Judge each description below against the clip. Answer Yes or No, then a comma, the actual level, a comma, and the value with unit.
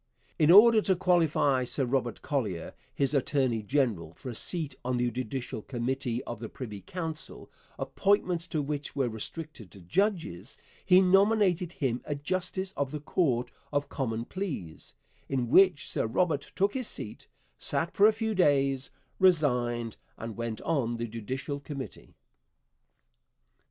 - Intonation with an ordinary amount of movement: No, wide, 6.8 semitones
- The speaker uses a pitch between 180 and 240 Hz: No, medium, 140 Hz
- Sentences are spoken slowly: No, average, 145 wpm